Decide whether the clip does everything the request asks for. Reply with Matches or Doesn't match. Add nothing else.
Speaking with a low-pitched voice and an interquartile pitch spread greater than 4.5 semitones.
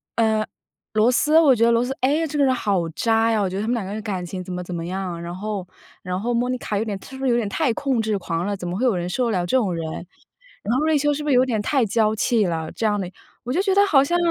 Doesn't match